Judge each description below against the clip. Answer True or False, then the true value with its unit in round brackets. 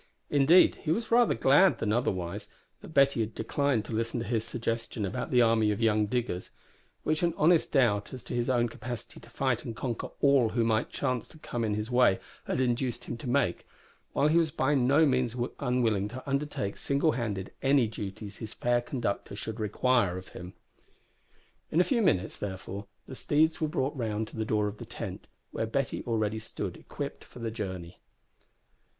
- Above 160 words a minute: True (190 wpm)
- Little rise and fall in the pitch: False (4.1 semitones)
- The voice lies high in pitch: False (120 Hz)